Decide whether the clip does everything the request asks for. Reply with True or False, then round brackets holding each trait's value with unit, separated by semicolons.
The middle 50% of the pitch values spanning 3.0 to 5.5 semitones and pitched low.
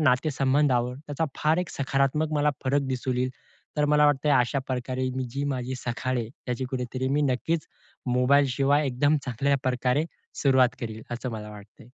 False (2.4 semitones; 130 Hz)